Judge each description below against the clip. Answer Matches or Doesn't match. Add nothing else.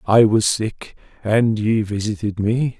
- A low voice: Matches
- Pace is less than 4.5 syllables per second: Matches